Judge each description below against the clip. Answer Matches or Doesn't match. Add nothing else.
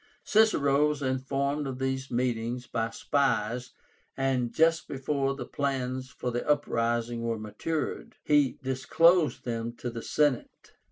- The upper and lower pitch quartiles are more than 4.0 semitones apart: Doesn't match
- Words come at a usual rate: Doesn't match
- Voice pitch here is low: Matches